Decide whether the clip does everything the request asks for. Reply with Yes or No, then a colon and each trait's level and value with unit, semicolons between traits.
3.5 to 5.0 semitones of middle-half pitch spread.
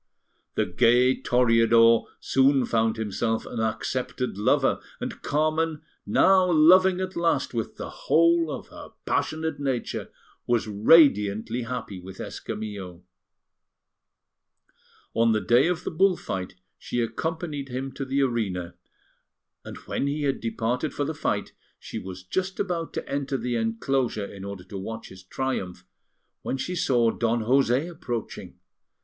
No: wide, 5.5 semitones